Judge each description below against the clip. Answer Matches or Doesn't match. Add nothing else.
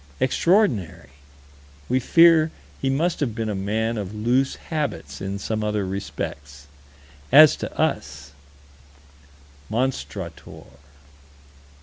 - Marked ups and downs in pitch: Matches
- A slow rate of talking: Matches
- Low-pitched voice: Matches